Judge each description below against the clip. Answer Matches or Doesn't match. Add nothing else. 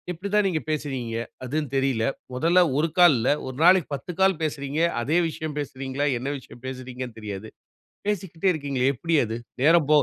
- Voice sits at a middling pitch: Matches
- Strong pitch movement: Doesn't match